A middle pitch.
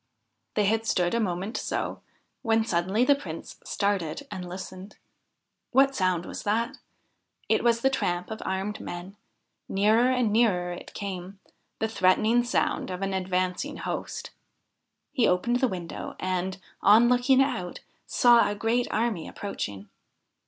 No: high, 205 Hz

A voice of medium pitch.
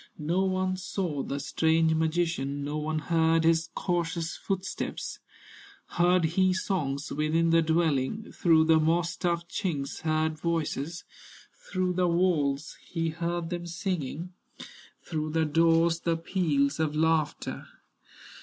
Yes: medium, 165 Hz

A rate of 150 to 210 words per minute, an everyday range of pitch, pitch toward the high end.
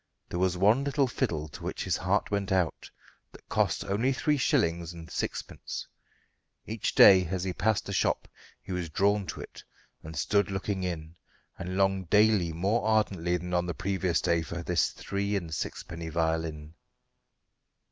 No: average, 165 wpm; average, 3.3 semitones; very low, 95 Hz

